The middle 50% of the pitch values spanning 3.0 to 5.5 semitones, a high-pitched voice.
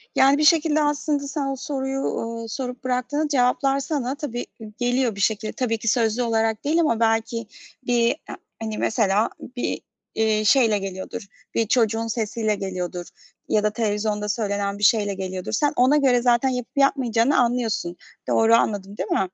Yes: average, 3.8 semitones; high, 230 Hz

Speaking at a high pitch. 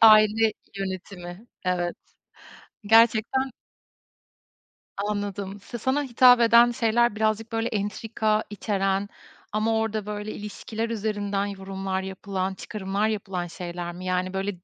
Yes: high, 205 Hz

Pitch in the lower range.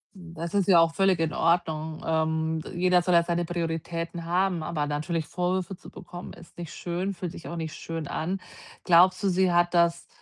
No: medium, 170 Hz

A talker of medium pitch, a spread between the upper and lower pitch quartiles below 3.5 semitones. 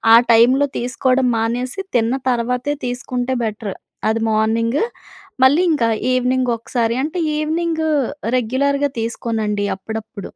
No: high, 245 Hz; average, 2.8 semitones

